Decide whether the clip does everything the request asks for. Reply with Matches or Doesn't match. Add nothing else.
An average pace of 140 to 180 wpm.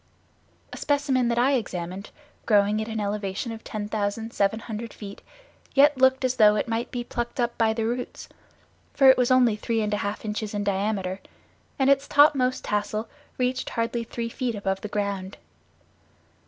Matches